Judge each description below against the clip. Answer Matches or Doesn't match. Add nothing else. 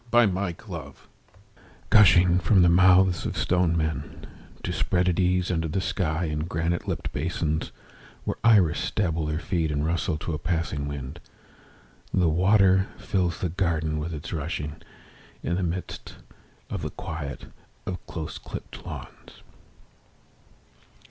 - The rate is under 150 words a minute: Matches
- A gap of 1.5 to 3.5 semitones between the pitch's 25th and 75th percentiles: Matches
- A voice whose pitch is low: Matches